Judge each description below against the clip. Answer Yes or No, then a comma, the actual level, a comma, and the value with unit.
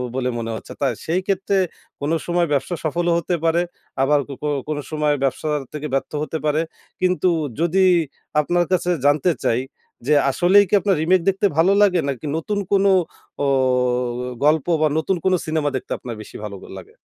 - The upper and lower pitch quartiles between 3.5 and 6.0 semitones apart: Yes, average, 3.9 semitones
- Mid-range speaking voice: Yes, medium, 160 Hz